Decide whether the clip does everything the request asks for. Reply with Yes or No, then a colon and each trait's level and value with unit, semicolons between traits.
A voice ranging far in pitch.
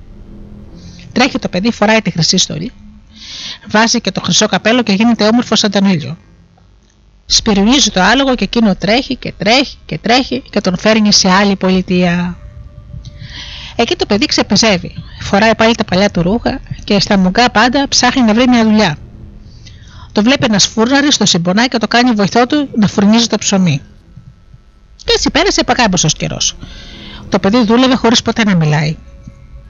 Yes: wide, 6.5 semitones